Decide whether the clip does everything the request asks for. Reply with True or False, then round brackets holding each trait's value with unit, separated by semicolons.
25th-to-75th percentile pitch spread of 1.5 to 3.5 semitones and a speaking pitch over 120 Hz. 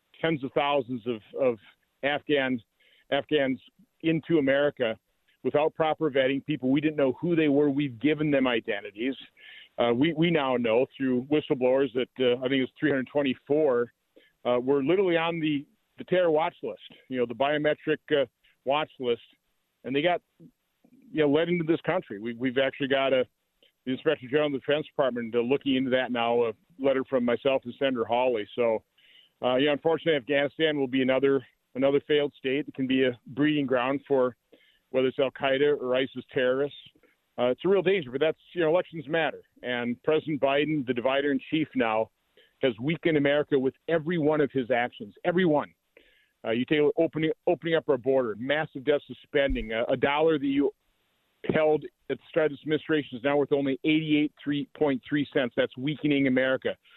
True (2.9 semitones; 140 Hz)